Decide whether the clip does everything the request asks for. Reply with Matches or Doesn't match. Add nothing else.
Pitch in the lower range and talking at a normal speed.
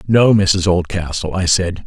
Matches